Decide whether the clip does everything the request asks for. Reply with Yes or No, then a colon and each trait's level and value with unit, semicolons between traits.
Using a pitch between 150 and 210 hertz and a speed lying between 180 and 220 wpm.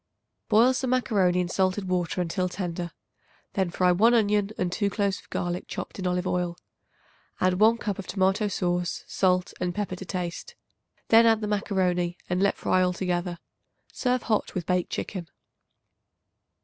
No: medium, 185 Hz; average, 160 wpm